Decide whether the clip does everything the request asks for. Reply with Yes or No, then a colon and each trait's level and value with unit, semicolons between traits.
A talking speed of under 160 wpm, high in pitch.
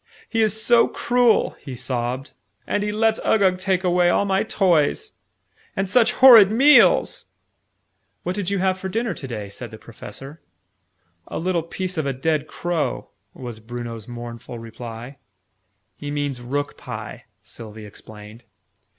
No: average, 150 wpm; medium, 165 Hz